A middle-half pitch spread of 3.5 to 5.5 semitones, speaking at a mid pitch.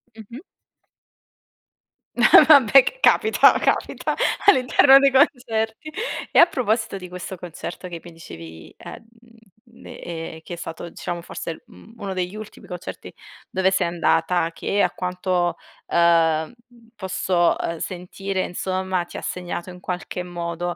Yes: average, 4.0 semitones; medium, 180 Hz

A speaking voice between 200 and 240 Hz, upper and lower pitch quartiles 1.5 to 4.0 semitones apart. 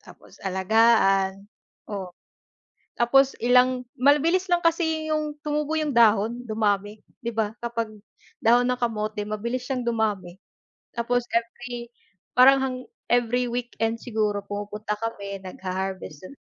Yes: high, 230 Hz; average, 3.4 semitones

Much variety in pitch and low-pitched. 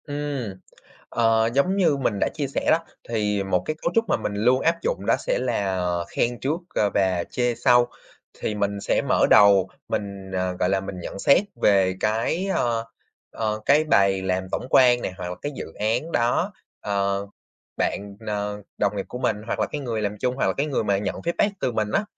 No: average, 4.9 semitones; low, 110 Hz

